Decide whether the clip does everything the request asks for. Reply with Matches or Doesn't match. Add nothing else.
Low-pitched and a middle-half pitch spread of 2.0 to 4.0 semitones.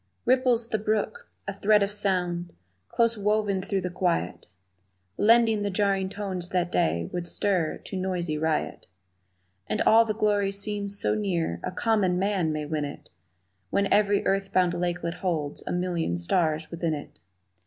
Doesn't match